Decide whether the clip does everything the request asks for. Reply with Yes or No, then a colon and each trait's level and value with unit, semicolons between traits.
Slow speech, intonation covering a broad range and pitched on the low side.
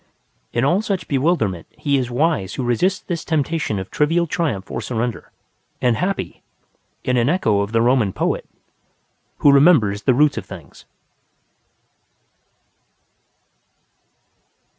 Yes: slow, 125 wpm; wide, 6.7 semitones; low, 130 Hz